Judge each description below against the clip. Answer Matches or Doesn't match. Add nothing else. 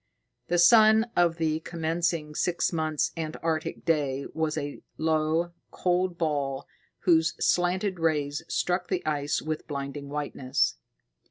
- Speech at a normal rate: Doesn't match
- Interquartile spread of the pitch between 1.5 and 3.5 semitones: Matches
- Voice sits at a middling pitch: Matches